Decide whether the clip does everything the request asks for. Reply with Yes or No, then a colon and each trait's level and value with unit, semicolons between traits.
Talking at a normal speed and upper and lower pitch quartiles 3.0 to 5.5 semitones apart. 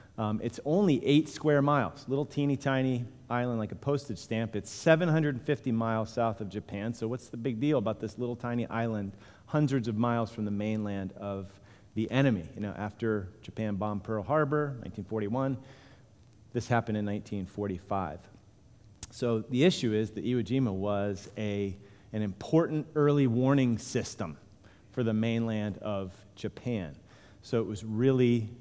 Yes: average, 155 wpm; average, 3.6 semitones